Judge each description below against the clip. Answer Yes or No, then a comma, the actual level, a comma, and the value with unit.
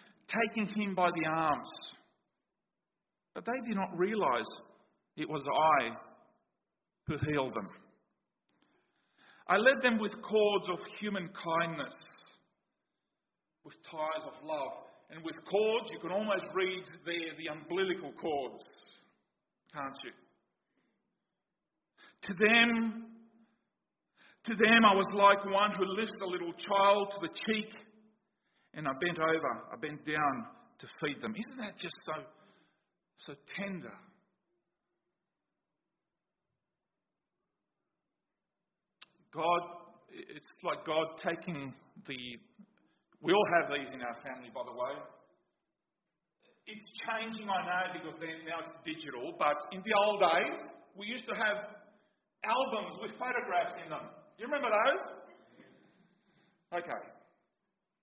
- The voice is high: Yes, high, 195 Hz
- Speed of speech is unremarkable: No, slow, 120 wpm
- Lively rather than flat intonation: No, average, 4.0 semitones